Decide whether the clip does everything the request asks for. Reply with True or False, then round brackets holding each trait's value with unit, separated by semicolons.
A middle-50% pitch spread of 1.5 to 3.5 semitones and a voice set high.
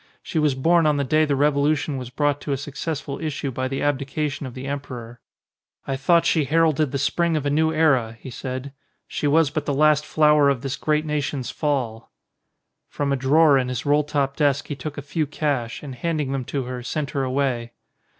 False (2.4 semitones; 140 Hz)